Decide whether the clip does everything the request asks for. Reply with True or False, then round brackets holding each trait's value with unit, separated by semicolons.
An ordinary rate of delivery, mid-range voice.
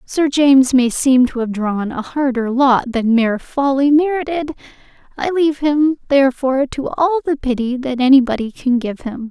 False (175 wpm; 265 Hz)